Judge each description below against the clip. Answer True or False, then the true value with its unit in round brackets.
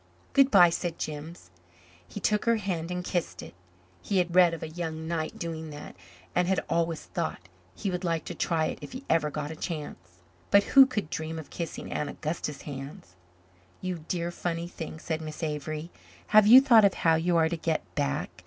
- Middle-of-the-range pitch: True (165 Hz)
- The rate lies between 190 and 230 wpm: True (200 wpm)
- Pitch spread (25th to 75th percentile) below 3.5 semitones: True (2.4 semitones)